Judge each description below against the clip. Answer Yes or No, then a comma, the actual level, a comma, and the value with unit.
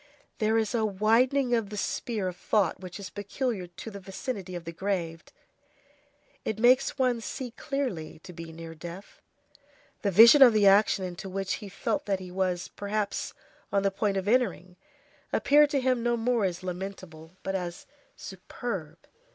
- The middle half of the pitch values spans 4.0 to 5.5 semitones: Yes, average, 4.3 semitones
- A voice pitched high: Yes, high, 200 Hz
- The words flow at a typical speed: Yes, average, 170 wpm